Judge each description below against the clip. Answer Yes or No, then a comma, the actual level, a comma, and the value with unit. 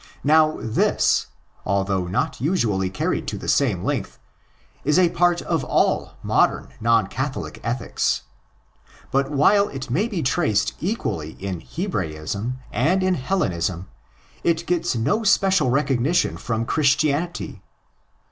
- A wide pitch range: Yes, wide, 8.7 semitones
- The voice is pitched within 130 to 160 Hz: Yes, low, 135 Hz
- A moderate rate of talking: No, slow, 130 wpm